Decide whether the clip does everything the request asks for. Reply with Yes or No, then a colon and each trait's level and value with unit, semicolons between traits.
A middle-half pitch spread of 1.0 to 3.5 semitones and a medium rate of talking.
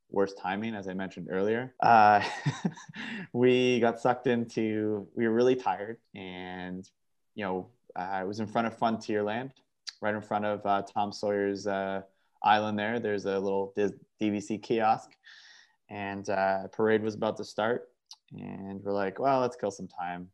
Yes: average, 3.0 semitones; average, 160 wpm